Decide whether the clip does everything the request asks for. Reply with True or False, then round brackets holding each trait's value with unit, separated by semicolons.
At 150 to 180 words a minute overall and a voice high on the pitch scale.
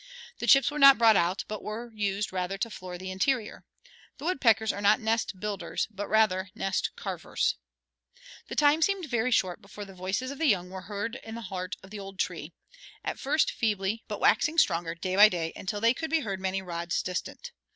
False (205 wpm; 205 Hz)